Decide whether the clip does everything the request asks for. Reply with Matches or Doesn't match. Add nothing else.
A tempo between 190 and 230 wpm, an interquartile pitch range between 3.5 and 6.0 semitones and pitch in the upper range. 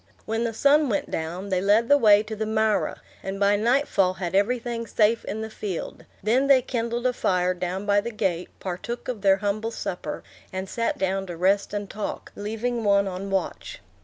Doesn't match